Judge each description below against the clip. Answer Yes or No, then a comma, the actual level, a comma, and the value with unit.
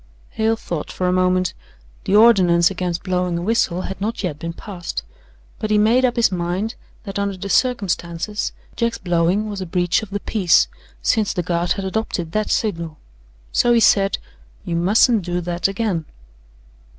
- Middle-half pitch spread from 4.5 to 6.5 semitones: No, average, 3.5 semitones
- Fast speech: No, average, 175 wpm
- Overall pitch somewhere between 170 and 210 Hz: Yes, high, 190 Hz